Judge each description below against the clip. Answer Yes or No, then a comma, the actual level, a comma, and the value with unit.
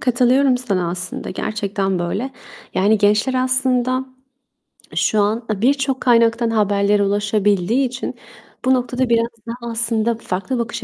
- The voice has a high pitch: Yes, high, 230 Hz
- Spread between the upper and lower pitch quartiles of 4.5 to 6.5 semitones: No, average, 3.6 semitones